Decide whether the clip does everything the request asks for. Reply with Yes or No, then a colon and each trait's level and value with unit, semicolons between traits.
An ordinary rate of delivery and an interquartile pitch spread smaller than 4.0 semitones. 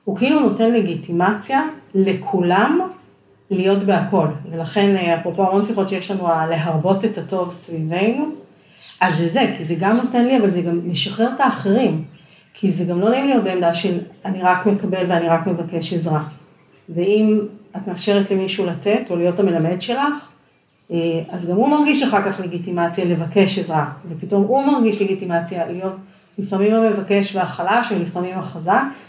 No: fast, 155 wpm; average, 3.2 semitones